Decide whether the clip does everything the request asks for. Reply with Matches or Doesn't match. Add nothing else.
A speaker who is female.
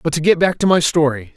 Doesn't match